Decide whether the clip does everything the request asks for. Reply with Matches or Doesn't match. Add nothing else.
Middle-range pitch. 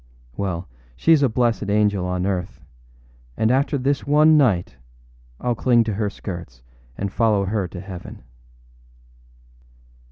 Doesn't match